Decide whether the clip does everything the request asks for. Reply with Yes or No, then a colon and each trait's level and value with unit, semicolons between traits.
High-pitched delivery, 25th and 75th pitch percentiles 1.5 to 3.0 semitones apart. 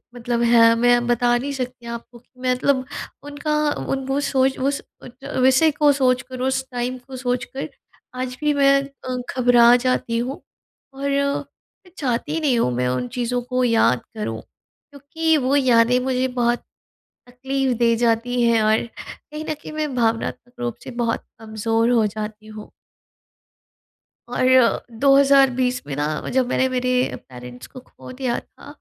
Yes: very high, 250 Hz; narrow, 2.4 semitones